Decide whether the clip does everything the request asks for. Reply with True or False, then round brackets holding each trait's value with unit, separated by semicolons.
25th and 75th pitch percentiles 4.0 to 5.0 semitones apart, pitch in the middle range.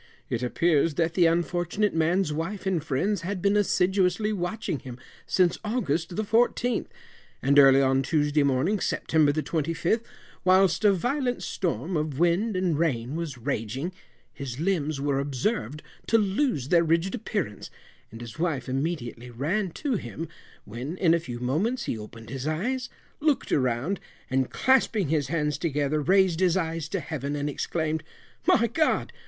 False (5.5 semitones; 165 Hz)